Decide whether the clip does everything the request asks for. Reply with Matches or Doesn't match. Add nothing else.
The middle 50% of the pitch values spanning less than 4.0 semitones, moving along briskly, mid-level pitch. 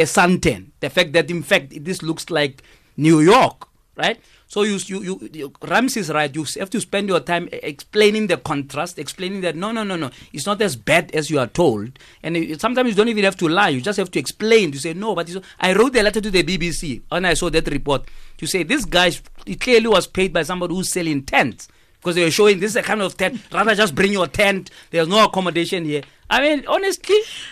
Doesn't match